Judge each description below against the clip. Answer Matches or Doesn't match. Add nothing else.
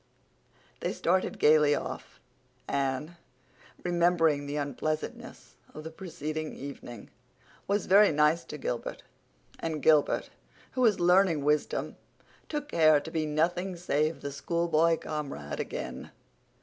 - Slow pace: Matches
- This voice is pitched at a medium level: Matches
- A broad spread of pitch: Doesn't match